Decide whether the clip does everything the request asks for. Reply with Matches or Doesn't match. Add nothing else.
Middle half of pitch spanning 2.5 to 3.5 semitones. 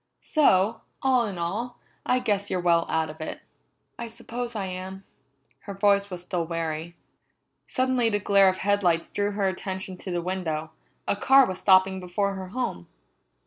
Matches